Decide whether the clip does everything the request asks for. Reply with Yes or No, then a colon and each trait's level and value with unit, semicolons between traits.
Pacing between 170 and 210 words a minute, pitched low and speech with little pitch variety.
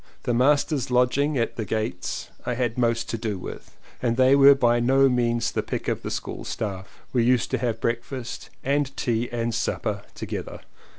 Yes: average, 185 wpm; low, 120 Hz; narrow, 2.0 semitones